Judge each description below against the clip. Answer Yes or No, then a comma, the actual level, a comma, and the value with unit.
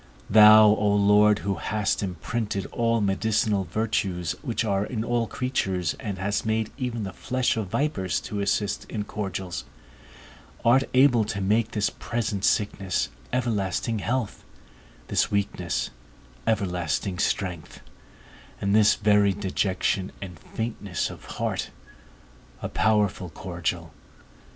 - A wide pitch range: No, average, 2.7 semitones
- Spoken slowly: Yes, slow, 120 wpm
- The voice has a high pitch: No, low, 105 Hz